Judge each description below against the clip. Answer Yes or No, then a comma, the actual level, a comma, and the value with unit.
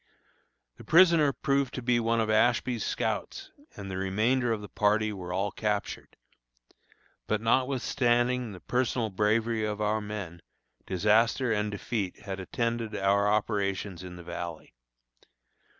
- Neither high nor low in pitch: No, low, 110 Hz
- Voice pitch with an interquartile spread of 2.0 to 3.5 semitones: Yes, average, 3.2 semitones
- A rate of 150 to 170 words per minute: No, slow, 135 wpm